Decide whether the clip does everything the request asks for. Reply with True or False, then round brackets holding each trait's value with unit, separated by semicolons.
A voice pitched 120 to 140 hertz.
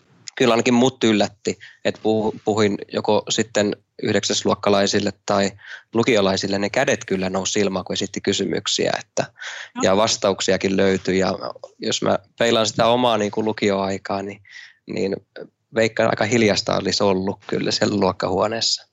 False (100 Hz)